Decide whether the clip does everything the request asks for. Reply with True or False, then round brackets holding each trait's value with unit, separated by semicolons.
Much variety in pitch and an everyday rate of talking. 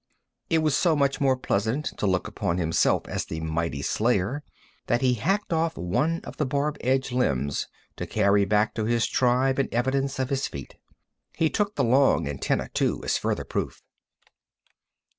True (5.9 semitones; 175 wpm)